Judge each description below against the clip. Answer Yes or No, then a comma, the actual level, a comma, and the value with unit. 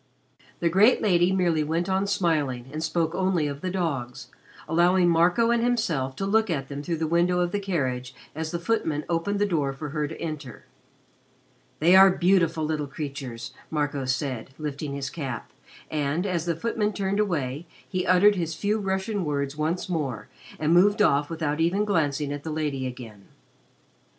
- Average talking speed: Yes, average, 175 wpm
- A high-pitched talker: No, medium, 160 Hz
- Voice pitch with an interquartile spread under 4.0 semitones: No, average, 4.5 semitones